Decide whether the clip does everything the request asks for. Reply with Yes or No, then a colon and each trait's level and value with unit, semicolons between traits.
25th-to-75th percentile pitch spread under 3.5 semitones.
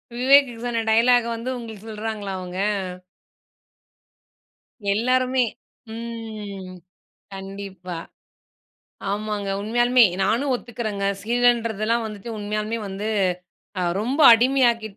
Yes: average, 2.9 semitones